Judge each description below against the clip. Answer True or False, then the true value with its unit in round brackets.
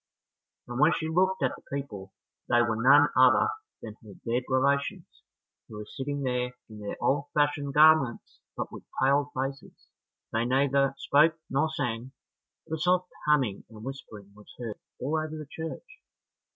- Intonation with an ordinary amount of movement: True (3.9 semitones)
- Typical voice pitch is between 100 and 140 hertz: True (135 Hz)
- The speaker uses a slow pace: False (165 wpm)